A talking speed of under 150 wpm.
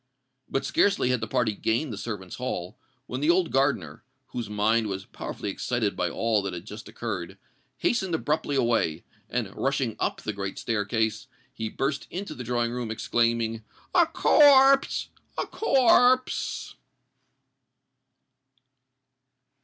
Yes: slow, 135 wpm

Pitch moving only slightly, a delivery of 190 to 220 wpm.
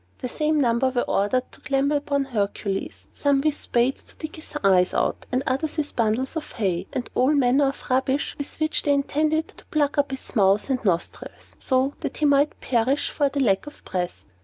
No: average, 3.5 semitones; average, 200 wpm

